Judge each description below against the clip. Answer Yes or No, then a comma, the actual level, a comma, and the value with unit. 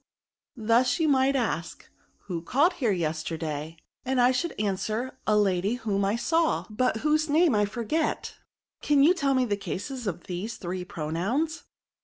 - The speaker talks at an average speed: Yes, average, 165 wpm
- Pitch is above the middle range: Yes, high, 225 Hz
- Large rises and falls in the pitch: Yes, wide, 6.4 semitones